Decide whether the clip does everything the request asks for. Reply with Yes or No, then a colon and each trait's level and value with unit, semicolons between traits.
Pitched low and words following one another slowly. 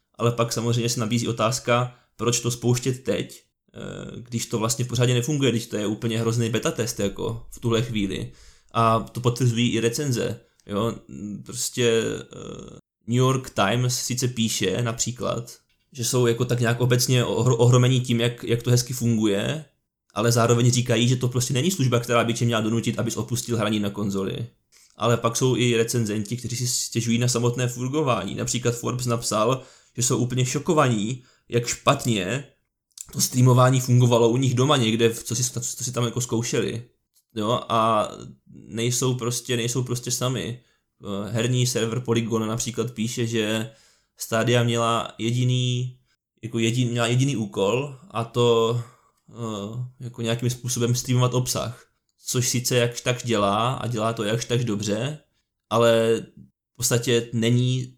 No: low, 120 Hz; average, 150 wpm